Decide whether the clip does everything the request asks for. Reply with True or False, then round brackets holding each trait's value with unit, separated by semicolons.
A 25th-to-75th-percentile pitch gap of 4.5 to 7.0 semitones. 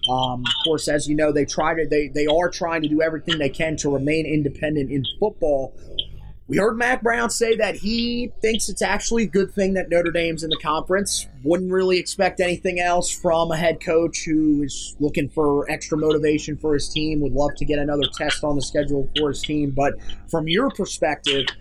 False (3.7 semitones)